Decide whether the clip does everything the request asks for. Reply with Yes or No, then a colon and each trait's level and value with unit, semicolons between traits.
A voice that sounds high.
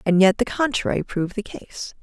Yes: high, 205 Hz